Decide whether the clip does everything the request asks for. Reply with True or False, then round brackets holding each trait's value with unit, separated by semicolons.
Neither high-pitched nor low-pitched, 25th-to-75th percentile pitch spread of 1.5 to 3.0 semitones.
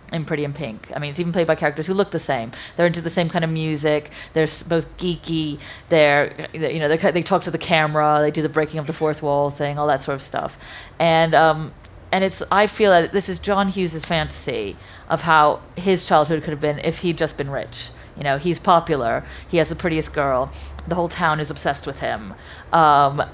True (160 Hz; 2.4 semitones)